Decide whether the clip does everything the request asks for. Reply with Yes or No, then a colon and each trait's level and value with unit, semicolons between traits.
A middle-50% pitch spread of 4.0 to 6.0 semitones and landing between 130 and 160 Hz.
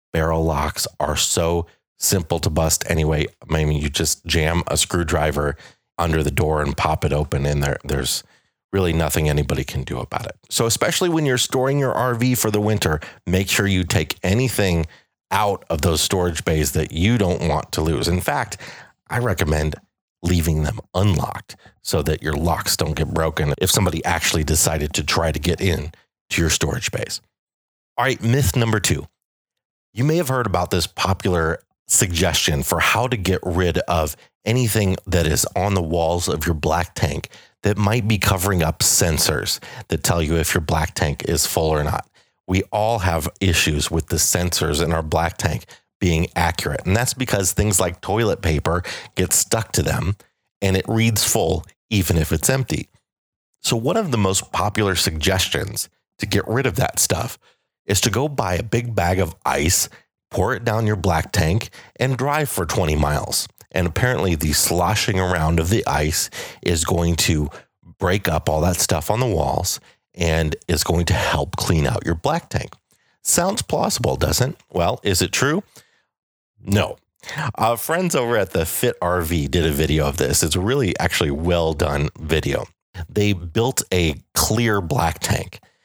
No: average, 4.5 semitones; very low, 90 Hz